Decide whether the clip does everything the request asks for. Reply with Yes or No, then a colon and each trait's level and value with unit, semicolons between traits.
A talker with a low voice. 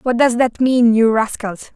No: high, 235 Hz